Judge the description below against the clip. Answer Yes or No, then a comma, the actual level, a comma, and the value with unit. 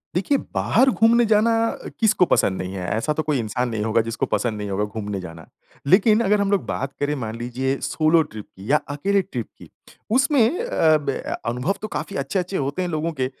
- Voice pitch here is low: No, medium, 145 Hz